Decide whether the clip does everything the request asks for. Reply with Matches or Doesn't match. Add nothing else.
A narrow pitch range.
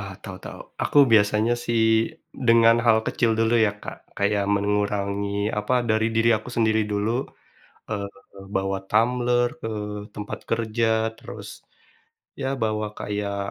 Matches